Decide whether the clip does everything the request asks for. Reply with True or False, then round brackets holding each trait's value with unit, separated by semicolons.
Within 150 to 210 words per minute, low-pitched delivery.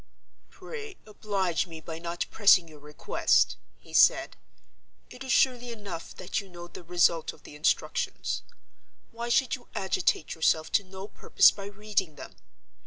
False (155 wpm; 190 Hz)